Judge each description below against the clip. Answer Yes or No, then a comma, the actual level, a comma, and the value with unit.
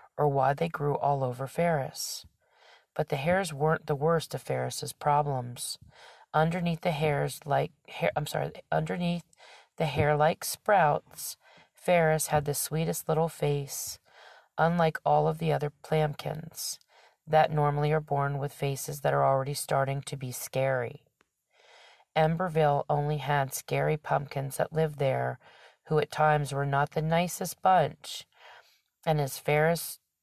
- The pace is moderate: Yes, average, 145 wpm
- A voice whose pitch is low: No, medium, 150 Hz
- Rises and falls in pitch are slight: Yes, narrow, 2.2 semitones